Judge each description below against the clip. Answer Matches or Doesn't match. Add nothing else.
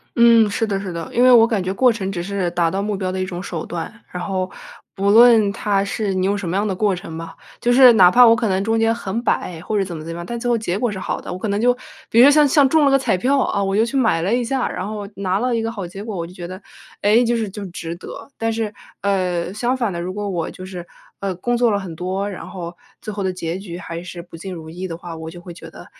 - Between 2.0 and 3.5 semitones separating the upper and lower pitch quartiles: Doesn't match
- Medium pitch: Doesn't match